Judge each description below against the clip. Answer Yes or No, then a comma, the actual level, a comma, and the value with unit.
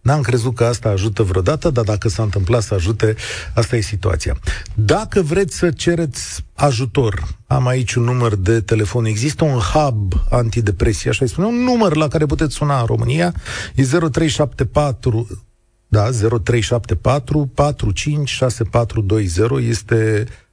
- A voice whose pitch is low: Yes, low, 120 Hz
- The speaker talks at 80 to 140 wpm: Yes, average, 135 wpm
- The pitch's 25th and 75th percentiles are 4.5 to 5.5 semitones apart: Yes, average, 4.8 semitones